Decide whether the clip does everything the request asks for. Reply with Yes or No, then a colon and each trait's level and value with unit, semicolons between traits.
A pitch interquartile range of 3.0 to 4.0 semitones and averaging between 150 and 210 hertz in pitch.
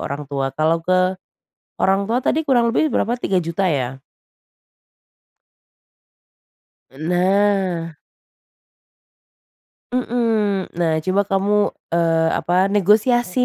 No: average, 4.5 semitones; high, 190 Hz